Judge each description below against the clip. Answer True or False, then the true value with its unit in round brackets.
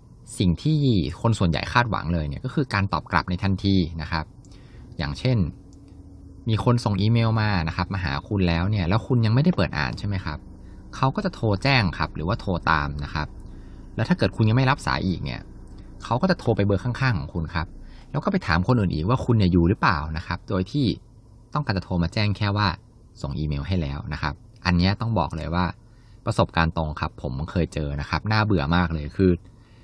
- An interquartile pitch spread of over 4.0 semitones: True (5.3 semitones)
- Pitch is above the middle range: False (95 Hz)